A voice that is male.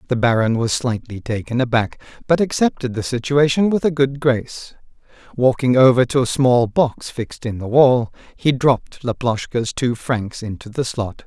Yes: male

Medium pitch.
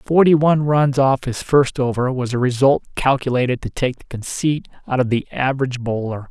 No: low, 130 Hz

